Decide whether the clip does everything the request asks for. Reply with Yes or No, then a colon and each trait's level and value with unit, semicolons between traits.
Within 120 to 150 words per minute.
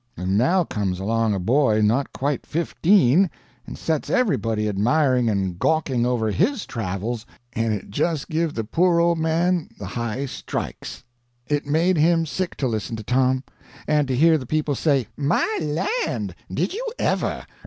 No: average, 165 wpm